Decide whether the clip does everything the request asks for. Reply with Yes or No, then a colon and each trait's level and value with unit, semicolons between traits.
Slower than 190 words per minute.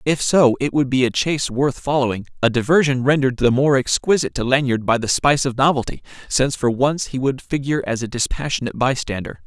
No: average, 195 wpm